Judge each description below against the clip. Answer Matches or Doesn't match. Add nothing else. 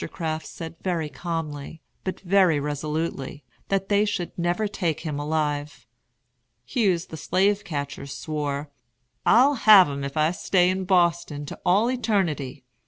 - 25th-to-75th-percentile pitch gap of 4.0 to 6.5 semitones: Matches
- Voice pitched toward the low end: Doesn't match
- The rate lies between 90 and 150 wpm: Matches